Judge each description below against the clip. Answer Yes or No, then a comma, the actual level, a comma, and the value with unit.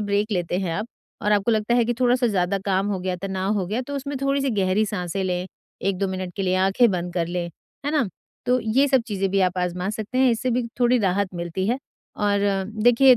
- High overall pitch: Yes, high, 200 Hz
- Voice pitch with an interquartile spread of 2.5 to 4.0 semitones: No, average, 4.6 semitones